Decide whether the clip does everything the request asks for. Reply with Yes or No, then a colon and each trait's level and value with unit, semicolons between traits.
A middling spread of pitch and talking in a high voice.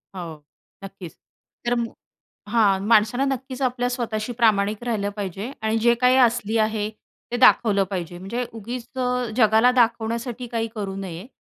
Yes: average, 3.2 semitones; high, 225 Hz